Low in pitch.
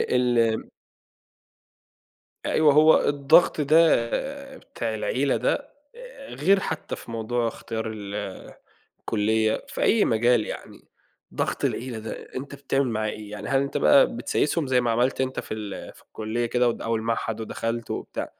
Yes: low, 120 Hz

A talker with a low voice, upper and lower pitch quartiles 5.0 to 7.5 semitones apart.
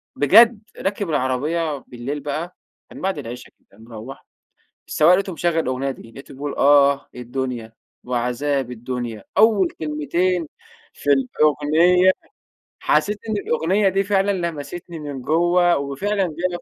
No: medium, 150 Hz; average, 5.3 semitones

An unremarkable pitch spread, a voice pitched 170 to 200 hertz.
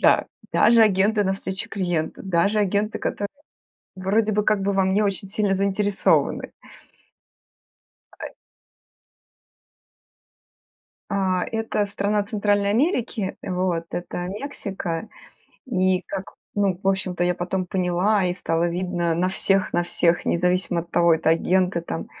No: narrow, 2.3 semitones; high, 190 Hz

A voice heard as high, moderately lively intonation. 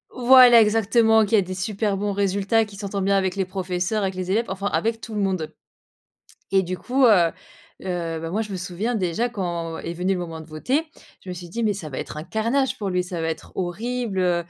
Yes: high, 195 Hz; average, 3.7 semitones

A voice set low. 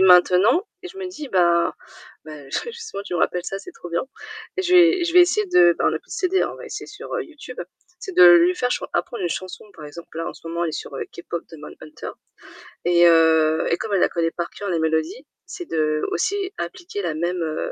No: medium, 180 Hz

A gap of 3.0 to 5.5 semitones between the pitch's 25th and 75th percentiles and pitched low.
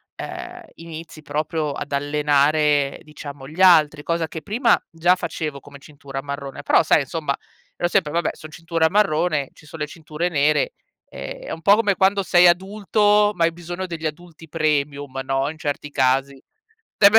No: average, 3.4 semitones; medium, 155 Hz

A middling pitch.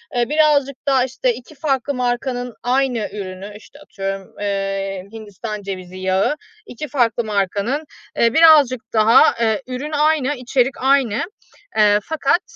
No: high, 245 Hz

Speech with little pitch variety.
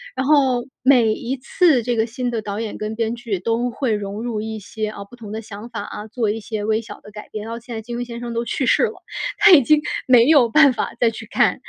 Yes: narrow, 2.3 semitones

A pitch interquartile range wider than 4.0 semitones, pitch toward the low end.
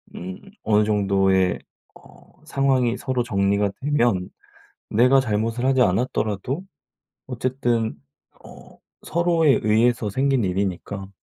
Yes: average, 4.7 semitones; low, 115 Hz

